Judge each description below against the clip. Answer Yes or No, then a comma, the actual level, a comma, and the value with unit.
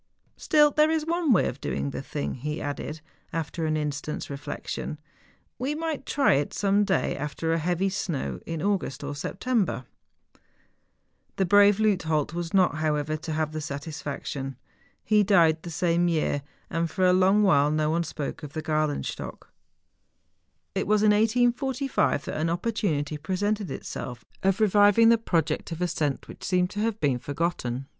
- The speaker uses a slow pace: No, average, 165 wpm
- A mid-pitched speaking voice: Yes, medium, 170 Hz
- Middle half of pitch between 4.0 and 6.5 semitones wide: Yes, wide, 5.5 semitones